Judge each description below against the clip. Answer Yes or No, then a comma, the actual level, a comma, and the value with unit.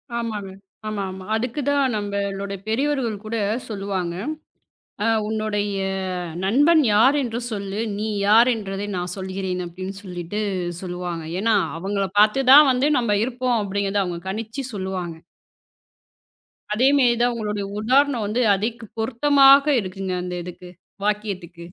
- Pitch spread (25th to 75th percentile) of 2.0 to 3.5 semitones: No, average, 3.9 semitones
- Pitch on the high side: Yes, high, 210 Hz